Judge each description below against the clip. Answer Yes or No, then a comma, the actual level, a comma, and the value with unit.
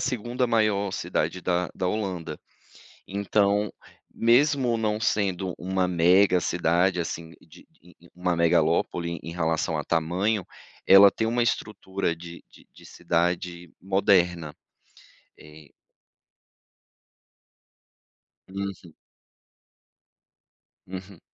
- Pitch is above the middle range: No, very low, 90 Hz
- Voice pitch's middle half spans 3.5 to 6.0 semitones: No, average, 3.1 semitones